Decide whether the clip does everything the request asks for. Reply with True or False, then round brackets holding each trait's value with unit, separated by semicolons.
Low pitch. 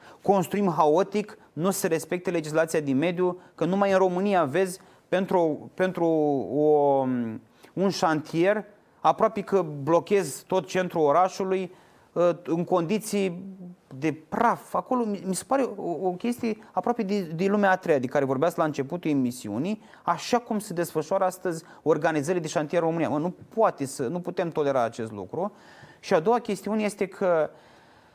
False (180 Hz)